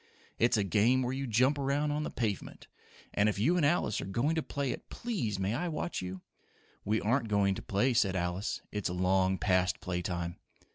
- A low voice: Yes, low, 110 Hz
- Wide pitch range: Yes, wide, 6.3 semitones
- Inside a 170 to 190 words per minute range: No, fast, 205 wpm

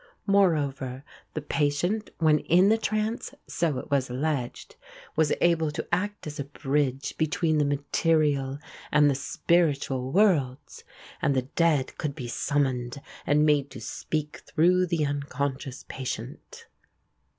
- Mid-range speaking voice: Yes, medium, 145 Hz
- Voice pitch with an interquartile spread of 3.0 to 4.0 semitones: Yes, average, 3.3 semitones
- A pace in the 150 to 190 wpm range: No, slow, 135 wpm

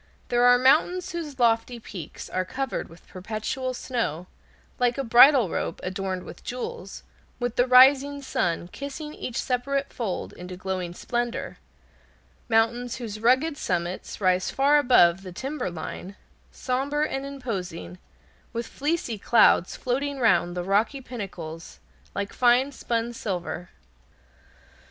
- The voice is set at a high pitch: Yes, high, 240 Hz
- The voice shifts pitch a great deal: Yes, wide, 6.1 semitones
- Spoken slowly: Yes, slow, 130 wpm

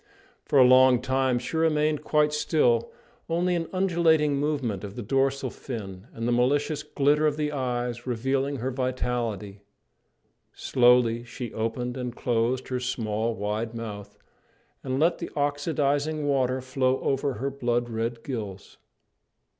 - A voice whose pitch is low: Yes, low, 130 Hz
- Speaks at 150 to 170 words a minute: No, average, 140 wpm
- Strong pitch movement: No, average, 3.5 semitones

